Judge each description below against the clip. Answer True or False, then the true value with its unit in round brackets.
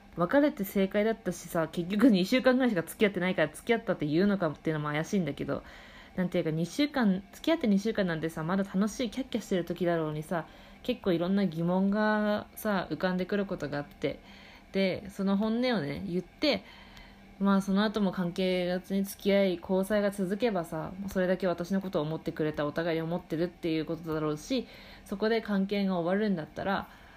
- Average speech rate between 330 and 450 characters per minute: True (420 characters per minute)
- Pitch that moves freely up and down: False (3.4 semitones)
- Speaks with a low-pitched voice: False (190 Hz)